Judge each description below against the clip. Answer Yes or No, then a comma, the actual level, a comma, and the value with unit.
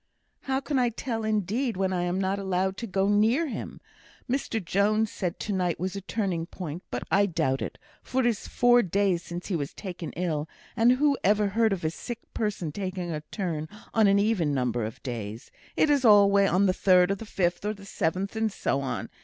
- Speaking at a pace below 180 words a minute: No, fast, 205 wpm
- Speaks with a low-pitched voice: No, high, 195 Hz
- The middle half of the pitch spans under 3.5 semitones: No, average, 4.0 semitones